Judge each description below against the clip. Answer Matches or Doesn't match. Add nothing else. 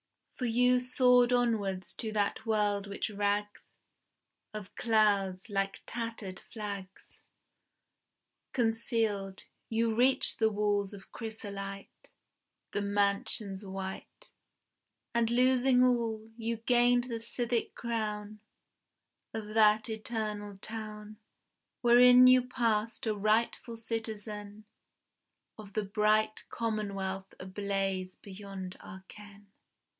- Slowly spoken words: Matches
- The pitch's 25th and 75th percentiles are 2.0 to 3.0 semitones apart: Matches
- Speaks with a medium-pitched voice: Doesn't match